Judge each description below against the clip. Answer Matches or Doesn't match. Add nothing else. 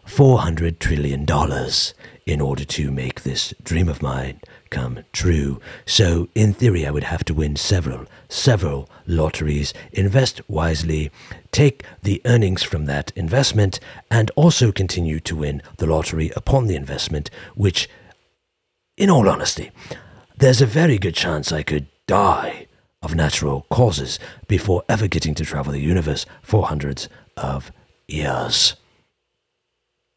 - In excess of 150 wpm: Doesn't match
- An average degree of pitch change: Doesn't match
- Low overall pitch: Matches